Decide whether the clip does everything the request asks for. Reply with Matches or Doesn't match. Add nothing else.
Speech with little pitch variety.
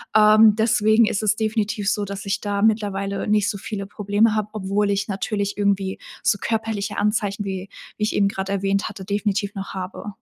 Matches